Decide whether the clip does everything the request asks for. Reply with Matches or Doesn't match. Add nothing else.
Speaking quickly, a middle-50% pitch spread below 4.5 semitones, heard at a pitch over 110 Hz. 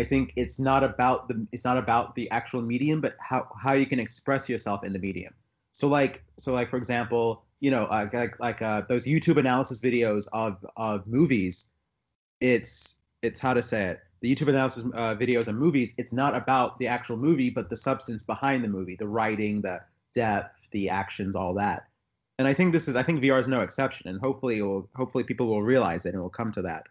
Matches